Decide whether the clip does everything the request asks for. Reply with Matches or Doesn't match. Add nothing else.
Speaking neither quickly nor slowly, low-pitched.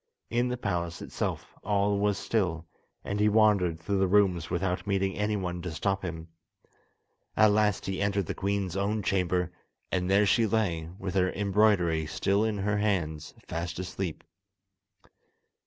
Matches